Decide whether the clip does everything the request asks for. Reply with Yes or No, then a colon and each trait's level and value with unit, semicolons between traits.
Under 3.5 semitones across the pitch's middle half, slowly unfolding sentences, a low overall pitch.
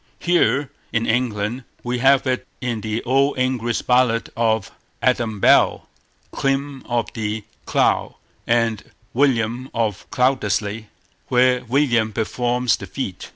Yes: narrow, 2.6 semitones; slow, 120 wpm; low, 120 Hz